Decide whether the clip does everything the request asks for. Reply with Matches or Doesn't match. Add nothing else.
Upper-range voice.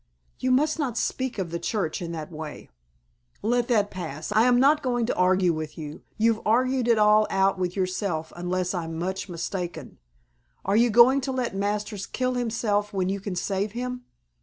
Matches